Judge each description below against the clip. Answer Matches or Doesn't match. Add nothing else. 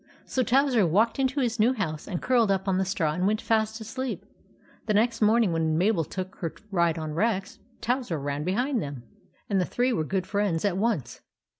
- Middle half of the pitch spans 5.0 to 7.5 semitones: Matches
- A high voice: Matches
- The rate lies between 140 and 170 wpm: Doesn't match